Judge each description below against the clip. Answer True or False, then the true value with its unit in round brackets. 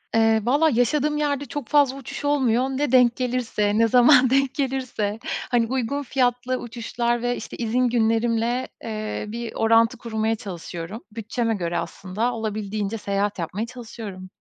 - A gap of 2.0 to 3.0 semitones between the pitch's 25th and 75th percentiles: True (2.6 semitones)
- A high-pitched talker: True (235 Hz)